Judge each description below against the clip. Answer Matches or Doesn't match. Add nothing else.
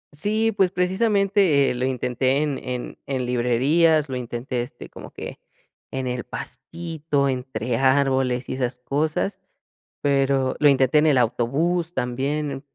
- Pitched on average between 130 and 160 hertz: Matches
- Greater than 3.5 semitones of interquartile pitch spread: Matches